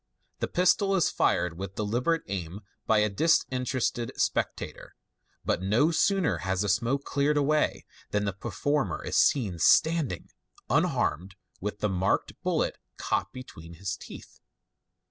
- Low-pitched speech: Yes, low, 110 Hz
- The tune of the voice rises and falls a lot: Yes, wide, 7.3 semitones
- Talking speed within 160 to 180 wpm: No, average, 140 wpm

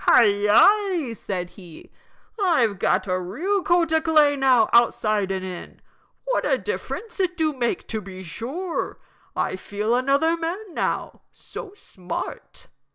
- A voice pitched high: Yes, very high, 260 Hz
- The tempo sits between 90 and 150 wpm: Yes, average, 145 wpm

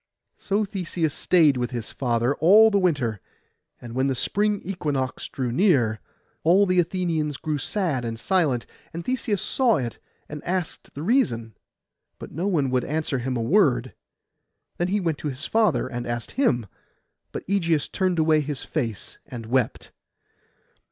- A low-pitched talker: No, medium, 155 Hz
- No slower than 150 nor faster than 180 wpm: Yes, average, 160 wpm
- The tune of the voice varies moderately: No, wide, 6.7 semitones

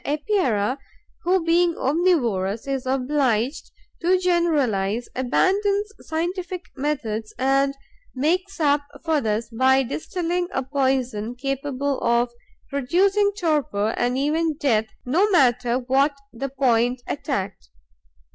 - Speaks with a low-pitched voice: No, very high, 275 Hz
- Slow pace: Yes, slow, 110 wpm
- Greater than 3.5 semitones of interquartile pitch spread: Yes, wide, 5.4 semitones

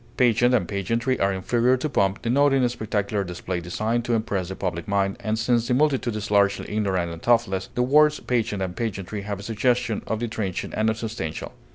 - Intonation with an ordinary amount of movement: Yes, average, 3.7 semitones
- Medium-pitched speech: No, low, 110 Hz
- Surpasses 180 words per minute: Yes, average, 195 wpm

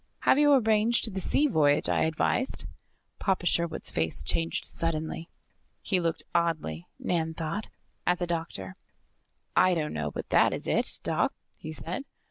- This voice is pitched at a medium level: Yes, medium, 165 Hz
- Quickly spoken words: No, average, 150 wpm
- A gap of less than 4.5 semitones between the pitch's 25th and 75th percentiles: Yes, average, 3.5 semitones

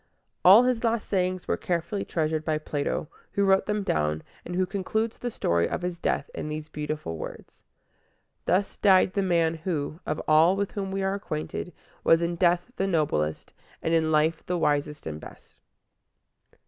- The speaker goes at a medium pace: Yes, average, 175 wpm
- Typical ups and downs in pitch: Yes, average, 4.0 semitones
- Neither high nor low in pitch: Yes, medium, 170 Hz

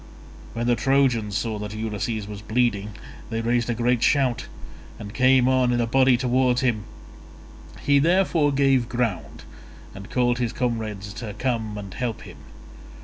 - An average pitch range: Yes, average, 3.1 semitones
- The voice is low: Yes, low, 120 Hz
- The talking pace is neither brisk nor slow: Yes, average, 155 wpm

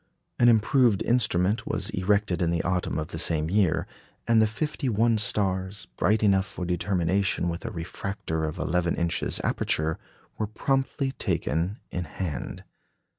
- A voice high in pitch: No, very low, 95 Hz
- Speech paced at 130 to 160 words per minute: Yes, average, 150 wpm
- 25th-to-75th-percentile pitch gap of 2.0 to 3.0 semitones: No, average, 4.1 semitones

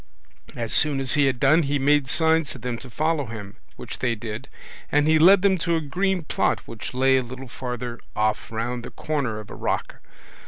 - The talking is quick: Yes, fast, 210 wpm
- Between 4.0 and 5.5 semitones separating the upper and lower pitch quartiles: Yes, average, 4.6 semitones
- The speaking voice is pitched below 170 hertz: Yes, low, 135 Hz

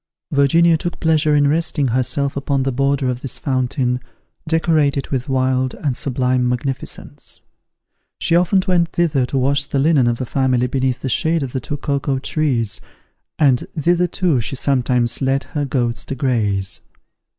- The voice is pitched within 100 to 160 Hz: Yes, low, 135 Hz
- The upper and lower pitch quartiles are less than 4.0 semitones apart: Yes, average, 2.8 semitones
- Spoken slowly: No, average, 160 wpm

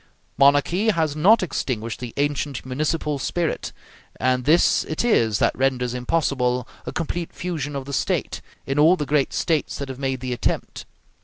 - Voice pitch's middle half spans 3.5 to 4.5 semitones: Yes, average, 3.9 semitones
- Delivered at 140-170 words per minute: Yes, average, 165 wpm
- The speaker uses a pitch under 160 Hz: Yes, medium, 140 Hz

